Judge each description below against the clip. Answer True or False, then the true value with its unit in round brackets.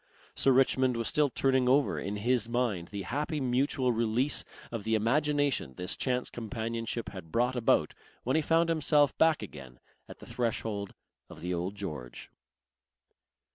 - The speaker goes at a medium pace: True (155 wpm)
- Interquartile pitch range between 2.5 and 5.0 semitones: True (4.6 semitones)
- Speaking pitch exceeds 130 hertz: False (120 Hz)